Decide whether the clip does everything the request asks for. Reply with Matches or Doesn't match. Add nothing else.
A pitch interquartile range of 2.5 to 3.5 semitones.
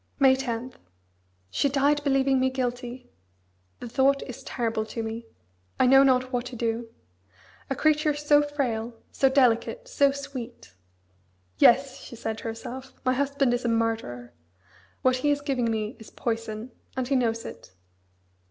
Matches